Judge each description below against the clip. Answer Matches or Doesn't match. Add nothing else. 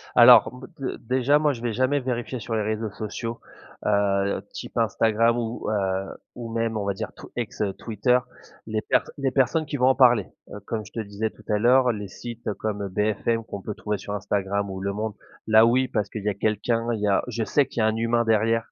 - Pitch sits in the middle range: Doesn't match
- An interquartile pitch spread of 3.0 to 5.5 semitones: Doesn't match